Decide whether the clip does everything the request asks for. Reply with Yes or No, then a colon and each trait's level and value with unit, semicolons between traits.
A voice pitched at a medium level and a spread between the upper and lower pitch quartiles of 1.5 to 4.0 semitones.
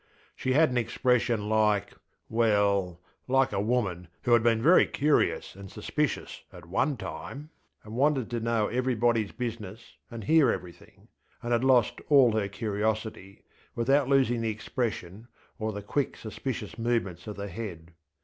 No: low, 115 Hz; average, 3.4 semitones